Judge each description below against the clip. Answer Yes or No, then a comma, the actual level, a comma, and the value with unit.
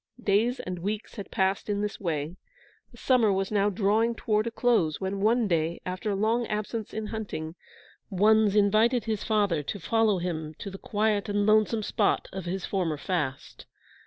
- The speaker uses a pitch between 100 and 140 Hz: No, high, 205 Hz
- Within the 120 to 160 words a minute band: No, average, 180 wpm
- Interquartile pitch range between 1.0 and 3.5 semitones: Yes, average, 2.9 semitones